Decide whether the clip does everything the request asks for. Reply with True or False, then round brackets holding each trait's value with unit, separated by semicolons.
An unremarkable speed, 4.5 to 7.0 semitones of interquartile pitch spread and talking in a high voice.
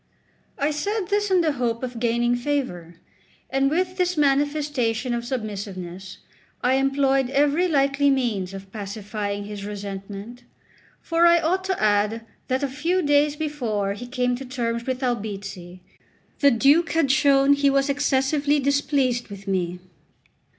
True (145 wpm; 5.4 semitones; 260 Hz)